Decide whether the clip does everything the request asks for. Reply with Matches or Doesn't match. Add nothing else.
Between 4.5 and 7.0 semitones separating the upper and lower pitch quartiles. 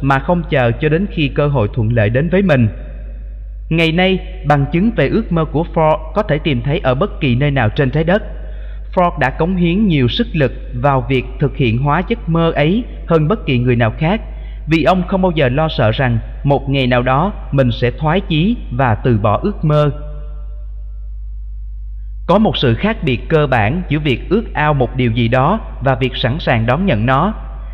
Matches